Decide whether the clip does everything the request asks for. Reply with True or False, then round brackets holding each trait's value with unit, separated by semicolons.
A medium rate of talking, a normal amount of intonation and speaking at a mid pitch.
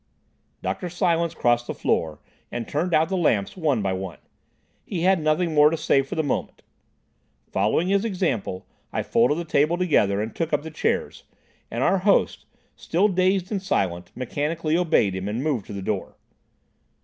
False (175 wpm; 7.4 semitones; 155 Hz)